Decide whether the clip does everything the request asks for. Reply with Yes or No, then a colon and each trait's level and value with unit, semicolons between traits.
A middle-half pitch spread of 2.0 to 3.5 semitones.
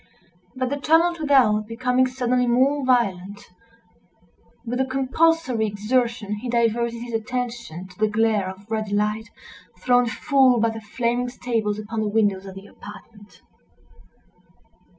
Yes: average, 3.1 semitones